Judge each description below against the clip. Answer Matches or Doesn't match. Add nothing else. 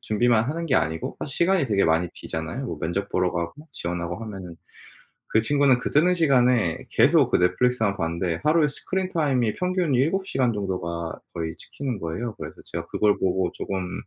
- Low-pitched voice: Matches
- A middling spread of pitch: Doesn't match